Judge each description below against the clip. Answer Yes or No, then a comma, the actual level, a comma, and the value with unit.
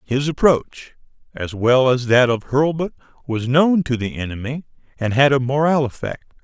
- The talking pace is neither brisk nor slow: Yes, average, 170 wpm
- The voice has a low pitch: Yes, low, 130 Hz